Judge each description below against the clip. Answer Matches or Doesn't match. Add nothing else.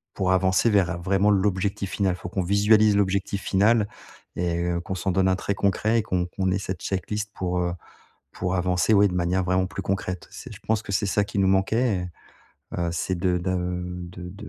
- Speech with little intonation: Matches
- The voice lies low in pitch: Matches